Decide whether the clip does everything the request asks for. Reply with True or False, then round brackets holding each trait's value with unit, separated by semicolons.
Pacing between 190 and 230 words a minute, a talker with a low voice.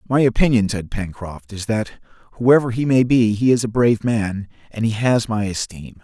True (200 wpm; 110 Hz)